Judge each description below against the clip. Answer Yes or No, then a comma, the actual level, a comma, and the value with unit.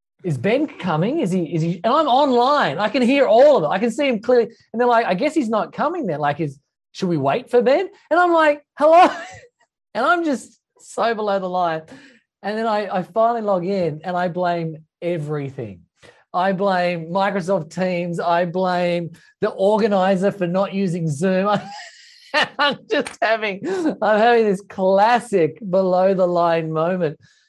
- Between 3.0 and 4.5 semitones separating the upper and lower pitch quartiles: No, average, 5.2 semitones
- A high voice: Yes, high, 195 Hz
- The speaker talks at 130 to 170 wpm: No, average, 180 wpm